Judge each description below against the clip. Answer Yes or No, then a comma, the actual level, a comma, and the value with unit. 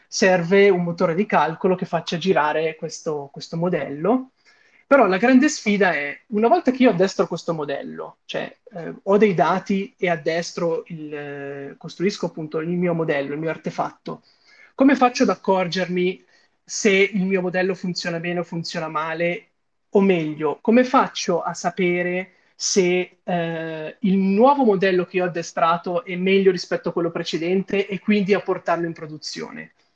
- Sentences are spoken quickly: No, average, 160 wpm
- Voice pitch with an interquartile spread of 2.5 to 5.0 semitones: Yes, average, 2.9 semitones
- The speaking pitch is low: No, medium, 180 Hz